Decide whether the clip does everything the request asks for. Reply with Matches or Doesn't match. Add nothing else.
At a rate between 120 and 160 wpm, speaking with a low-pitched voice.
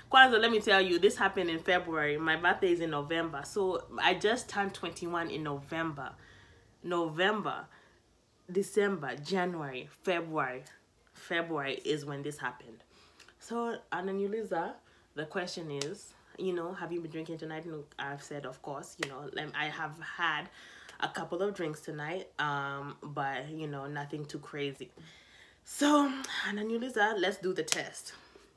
Doesn't match